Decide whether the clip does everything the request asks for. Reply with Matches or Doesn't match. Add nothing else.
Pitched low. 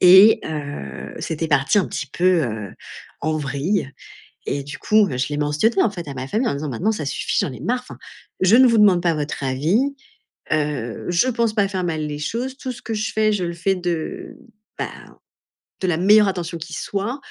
Doesn't match